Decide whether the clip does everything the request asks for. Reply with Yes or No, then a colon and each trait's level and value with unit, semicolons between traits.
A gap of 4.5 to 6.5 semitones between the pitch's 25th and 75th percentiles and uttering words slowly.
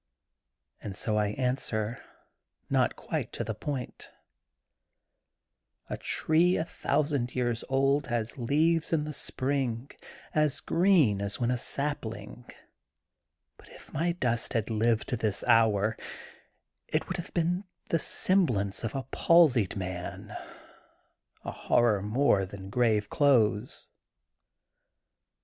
Yes: wide, 5.4 semitones; slow, 125 wpm